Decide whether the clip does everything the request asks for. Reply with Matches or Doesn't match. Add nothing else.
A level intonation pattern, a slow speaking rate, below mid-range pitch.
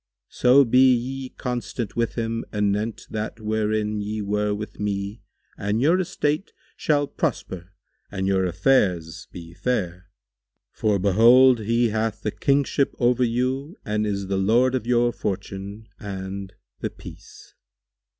Doesn't match